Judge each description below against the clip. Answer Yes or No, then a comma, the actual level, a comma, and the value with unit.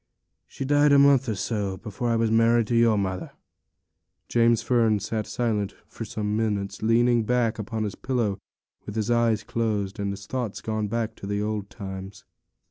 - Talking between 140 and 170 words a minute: No, average, 185 wpm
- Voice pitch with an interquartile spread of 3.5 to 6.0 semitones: No, narrow, 2.4 semitones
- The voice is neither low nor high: No, low, 110 Hz